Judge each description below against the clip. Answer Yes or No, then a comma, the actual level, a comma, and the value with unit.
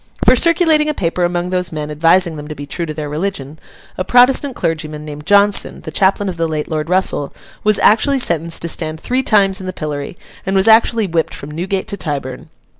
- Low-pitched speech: No, medium, 175 Hz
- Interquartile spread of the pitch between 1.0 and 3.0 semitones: No, average, 4.7 semitones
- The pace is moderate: No, fast, 210 wpm